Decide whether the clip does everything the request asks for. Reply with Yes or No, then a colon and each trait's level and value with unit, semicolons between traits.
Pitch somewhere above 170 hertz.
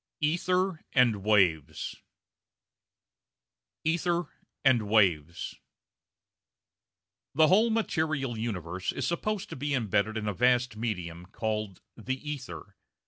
No: low, 120 Hz